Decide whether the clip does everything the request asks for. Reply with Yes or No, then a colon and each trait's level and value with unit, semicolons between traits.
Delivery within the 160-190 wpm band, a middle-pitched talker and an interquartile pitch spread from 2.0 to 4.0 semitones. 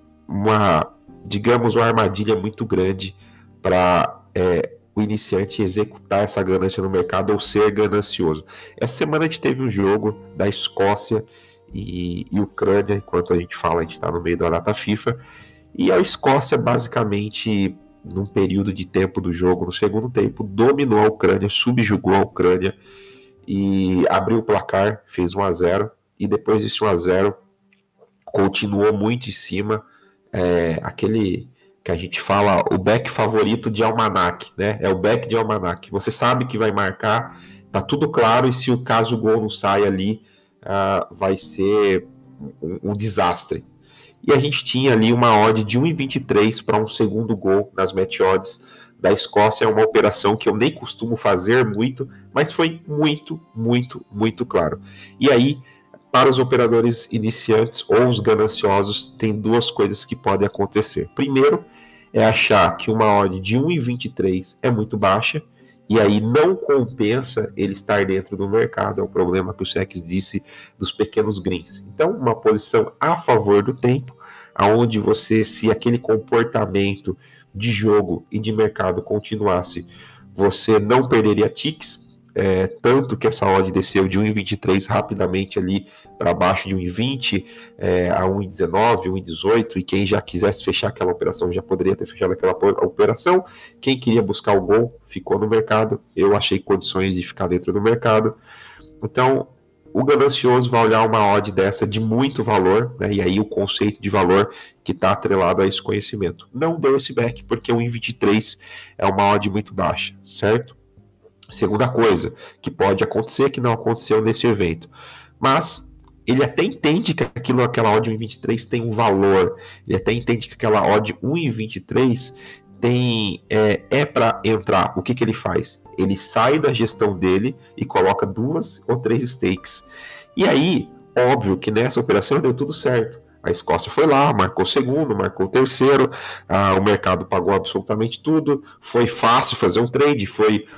No: average, 165 wpm; low, 105 Hz; average, 3.3 semitones